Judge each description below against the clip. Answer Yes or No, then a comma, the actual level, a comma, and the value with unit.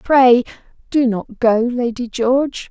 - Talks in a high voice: Yes, high, 245 Hz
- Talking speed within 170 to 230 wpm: No, slow, 135 wpm